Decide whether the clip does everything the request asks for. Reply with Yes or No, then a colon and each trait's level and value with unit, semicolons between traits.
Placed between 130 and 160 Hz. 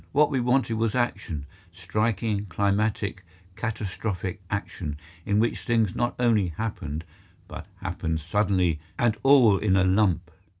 No: low, 100 Hz